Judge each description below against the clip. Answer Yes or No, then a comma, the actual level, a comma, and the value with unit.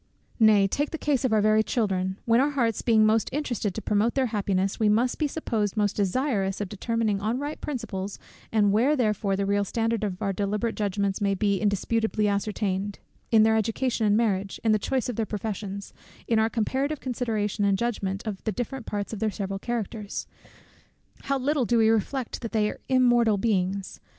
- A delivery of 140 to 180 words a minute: No, average, 195 wpm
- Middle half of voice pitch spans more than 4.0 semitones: No, average, 2.8 semitones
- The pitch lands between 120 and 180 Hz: No, high, 215 Hz